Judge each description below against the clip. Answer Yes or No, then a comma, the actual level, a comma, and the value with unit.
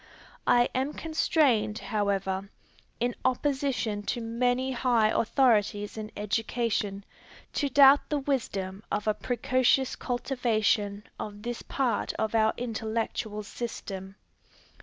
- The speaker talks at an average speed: No, slow, 110 wpm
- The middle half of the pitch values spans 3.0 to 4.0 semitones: Yes, average, 3.6 semitones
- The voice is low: No, high, 230 Hz